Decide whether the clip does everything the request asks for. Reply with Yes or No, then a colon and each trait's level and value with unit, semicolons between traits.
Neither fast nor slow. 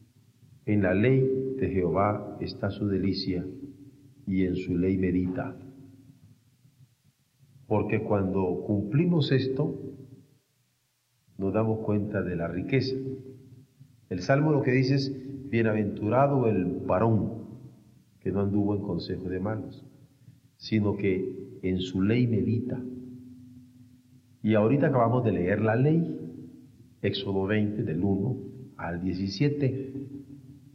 No: slow, 115 wpm